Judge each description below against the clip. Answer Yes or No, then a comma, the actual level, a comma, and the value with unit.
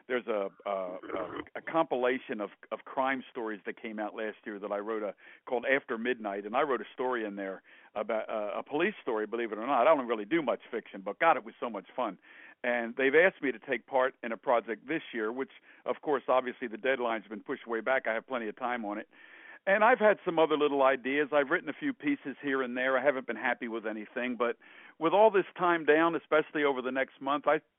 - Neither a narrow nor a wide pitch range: Yes, average, 4.3 semitones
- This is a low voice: Yes, low, 130 Hz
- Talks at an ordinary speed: No, fast, 245 wpm